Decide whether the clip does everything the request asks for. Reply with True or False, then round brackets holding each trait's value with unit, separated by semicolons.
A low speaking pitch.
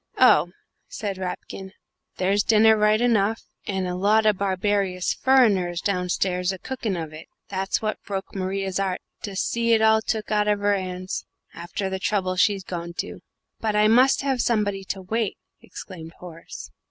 False (195 Hz)